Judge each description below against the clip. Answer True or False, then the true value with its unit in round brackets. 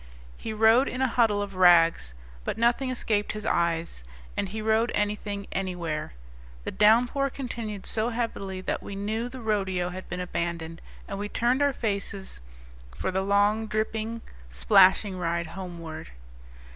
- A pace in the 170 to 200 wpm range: False (150 wpm)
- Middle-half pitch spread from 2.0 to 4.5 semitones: True (3.8 semitones)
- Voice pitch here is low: False (205 Hz)